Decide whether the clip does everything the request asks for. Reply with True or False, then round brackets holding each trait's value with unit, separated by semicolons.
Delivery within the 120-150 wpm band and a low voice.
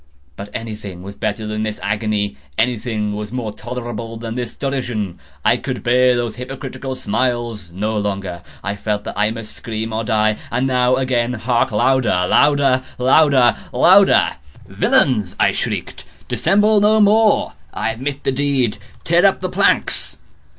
True (145 wpm; 120 Hz)